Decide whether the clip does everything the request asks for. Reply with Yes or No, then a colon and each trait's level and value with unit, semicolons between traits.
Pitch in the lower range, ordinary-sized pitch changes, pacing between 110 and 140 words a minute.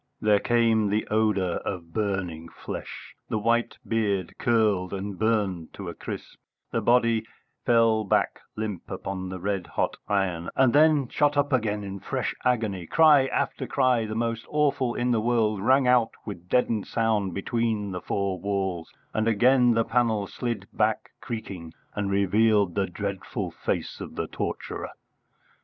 No: low, 110 Hz; average, 3.2 semitones; average, 155 wpm